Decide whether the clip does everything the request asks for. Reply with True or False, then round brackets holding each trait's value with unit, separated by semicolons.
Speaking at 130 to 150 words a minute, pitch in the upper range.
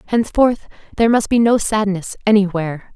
True (140 wpm; 210 Hz)